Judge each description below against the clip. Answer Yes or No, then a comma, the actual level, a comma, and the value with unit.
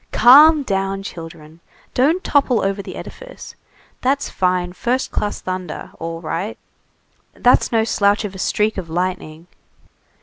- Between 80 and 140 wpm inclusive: Yes, slow, 135 wpm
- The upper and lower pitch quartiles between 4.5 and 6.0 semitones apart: Yes, wide, 5.5 semitones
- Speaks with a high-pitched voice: Yes, high, 195 Hz